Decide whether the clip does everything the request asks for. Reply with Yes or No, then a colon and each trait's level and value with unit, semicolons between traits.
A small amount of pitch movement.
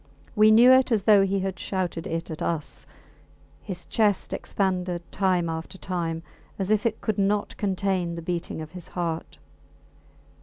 No: average, 3.2 semitones